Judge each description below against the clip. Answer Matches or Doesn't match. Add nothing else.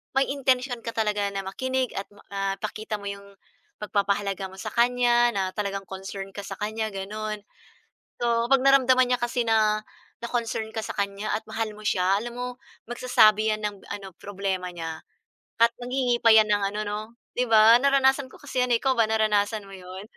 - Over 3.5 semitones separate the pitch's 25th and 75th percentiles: Doesn't match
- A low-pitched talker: Doesn't match